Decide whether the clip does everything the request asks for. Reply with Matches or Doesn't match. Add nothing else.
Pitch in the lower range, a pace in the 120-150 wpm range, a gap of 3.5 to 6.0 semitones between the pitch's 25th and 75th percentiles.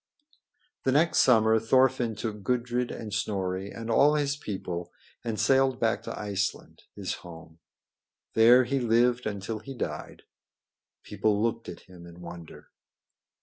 Matches